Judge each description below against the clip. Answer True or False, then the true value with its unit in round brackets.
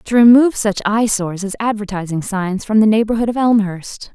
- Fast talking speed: False (175 wpm)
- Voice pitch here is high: True (210 Hz)